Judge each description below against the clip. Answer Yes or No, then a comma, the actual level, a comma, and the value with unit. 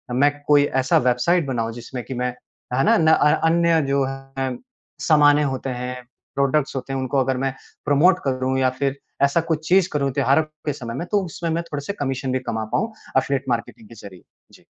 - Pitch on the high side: No, low, 135 Hz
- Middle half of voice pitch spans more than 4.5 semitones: No, narrow, 2.6 semitones